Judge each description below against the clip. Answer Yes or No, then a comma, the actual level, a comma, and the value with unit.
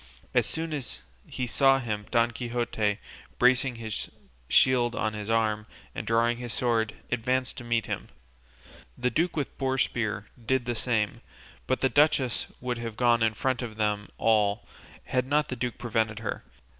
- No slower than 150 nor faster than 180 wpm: Yes, average, 170 wpm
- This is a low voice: Yes, low, 120 Hz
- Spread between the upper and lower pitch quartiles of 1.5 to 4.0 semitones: Yes, narrow, 2.5 semitones